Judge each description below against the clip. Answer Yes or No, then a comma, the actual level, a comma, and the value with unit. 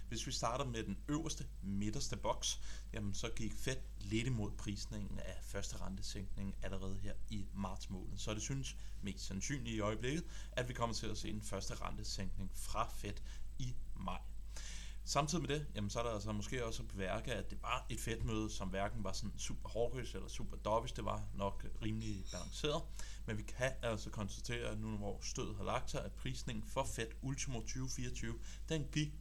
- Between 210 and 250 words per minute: No, average, 190 wpm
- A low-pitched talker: Yes, low, 110 Hz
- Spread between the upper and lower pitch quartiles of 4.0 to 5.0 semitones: No, average, 3.6 semitones